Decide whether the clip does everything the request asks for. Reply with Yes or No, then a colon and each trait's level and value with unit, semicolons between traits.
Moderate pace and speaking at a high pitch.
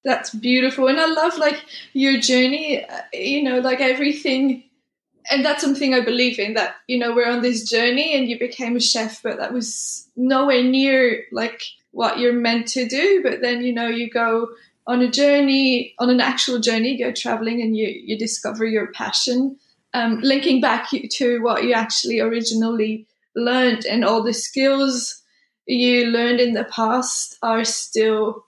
Yes: average, 175 wpm; high, 245 Hz